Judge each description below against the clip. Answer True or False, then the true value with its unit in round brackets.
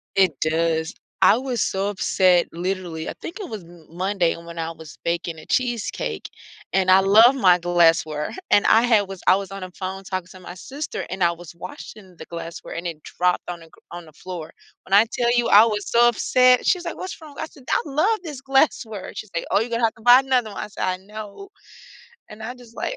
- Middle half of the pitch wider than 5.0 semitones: True (5.5 semitones)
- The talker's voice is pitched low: False (195 Hz)